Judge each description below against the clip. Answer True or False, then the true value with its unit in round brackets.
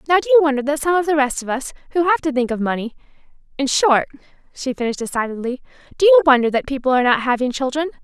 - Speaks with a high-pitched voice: True (275 Hz)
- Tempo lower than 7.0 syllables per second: False (7.3 syllables/s)